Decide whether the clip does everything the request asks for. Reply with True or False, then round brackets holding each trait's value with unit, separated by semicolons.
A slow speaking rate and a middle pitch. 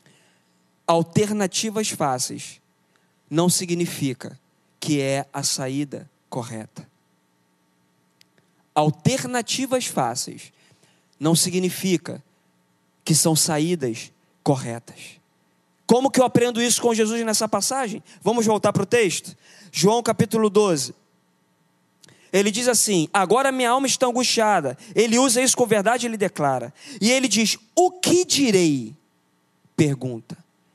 True (110 wpm; 175 Hz)